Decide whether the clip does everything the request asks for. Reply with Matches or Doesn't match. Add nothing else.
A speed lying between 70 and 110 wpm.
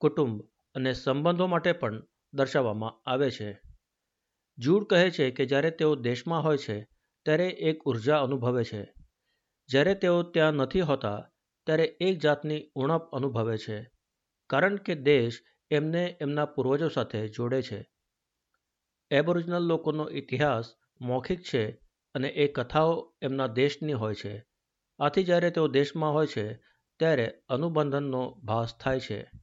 Doesn't match